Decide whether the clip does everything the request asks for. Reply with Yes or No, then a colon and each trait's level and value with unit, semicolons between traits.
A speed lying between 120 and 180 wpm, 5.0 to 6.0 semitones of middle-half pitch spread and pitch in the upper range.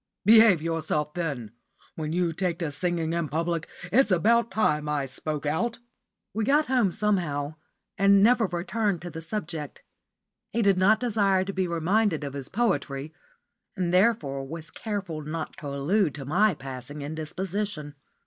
No: average, 155 wpm; average, 5.3 semitones; medium, 170 Hz